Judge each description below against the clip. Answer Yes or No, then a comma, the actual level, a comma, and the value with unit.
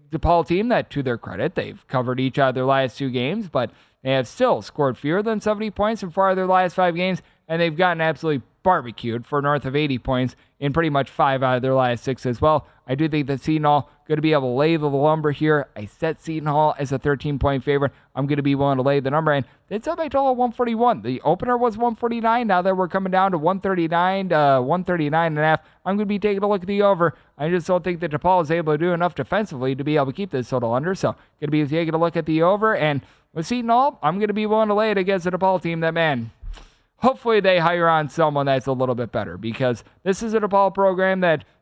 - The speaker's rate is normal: No, fast, 250 wpm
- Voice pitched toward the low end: No, medium, 160 Hz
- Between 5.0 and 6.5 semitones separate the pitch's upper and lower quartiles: Yes, wide, 5.5 semitones